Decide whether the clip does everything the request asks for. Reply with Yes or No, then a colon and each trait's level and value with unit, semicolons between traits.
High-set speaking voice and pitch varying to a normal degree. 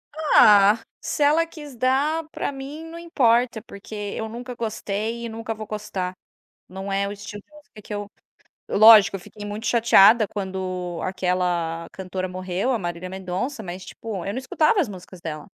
Yes: high, 210 Hz; average, 4.5 semitones